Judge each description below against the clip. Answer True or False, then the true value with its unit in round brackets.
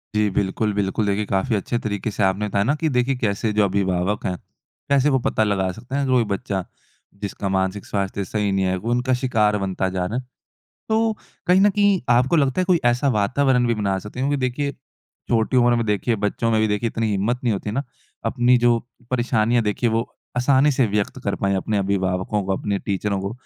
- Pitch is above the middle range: False (110 Hz)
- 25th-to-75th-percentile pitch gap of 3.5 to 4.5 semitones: True (4.1 semitones)